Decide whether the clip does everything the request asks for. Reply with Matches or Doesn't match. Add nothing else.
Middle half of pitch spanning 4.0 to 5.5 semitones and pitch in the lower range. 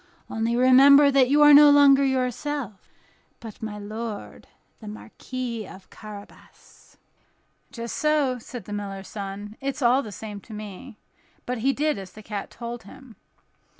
Doesn't match